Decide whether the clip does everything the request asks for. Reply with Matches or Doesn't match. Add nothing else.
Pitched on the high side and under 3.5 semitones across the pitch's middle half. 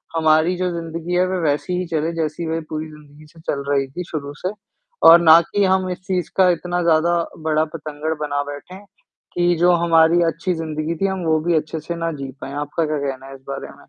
Doesn't match